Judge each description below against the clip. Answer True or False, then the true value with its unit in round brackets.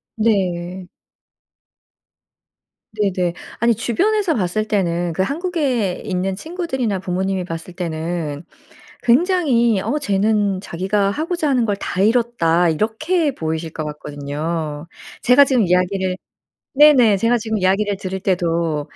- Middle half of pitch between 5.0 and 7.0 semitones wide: True (5.4 semitones)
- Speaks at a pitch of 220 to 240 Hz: False (195 Hz)